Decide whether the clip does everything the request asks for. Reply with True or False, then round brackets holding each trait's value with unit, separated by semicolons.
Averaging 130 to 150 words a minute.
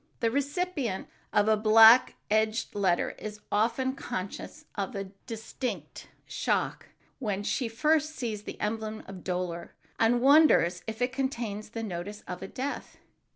True (145 wpm)